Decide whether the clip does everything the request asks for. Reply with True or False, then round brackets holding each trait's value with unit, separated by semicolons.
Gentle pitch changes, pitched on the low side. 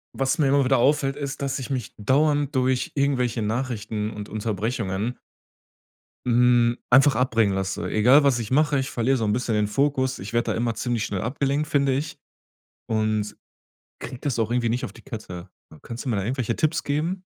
False (3.8 semitones; 125 Hz)